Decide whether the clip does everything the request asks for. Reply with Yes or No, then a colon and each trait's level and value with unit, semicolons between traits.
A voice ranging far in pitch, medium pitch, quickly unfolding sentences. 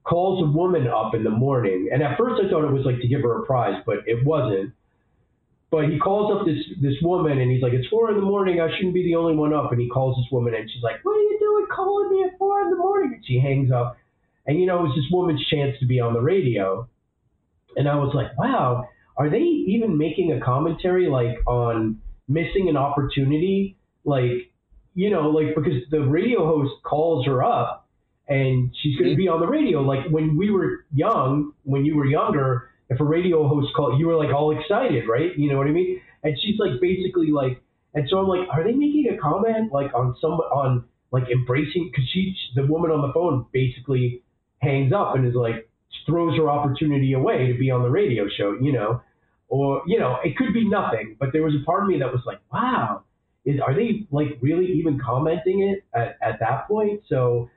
Yes: wide, 5.7 semitones; medium, 145 Hz; fast, 225 wpm